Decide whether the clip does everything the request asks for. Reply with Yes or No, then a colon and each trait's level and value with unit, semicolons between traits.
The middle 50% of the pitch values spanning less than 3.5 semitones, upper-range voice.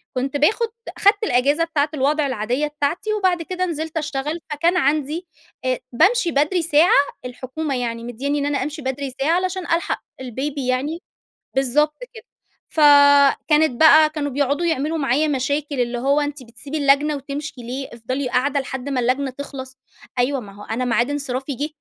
Yes: average, 2.9 semitones; very high, 285 Hz